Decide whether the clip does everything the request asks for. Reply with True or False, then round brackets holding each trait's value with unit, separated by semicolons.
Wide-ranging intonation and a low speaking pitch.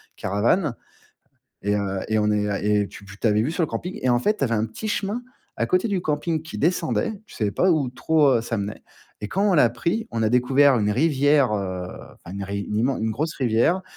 True (7.4 semitones; 125 Hz)